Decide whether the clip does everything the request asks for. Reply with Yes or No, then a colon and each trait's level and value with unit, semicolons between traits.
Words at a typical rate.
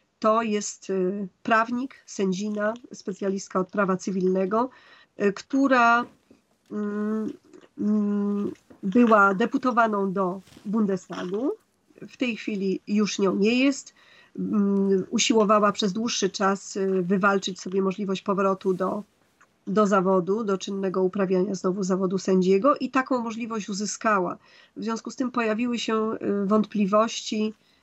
No: slow, 105 wpm